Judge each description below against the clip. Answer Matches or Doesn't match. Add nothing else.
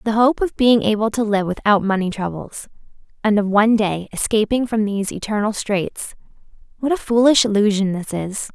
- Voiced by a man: Doesn't match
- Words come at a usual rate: Matches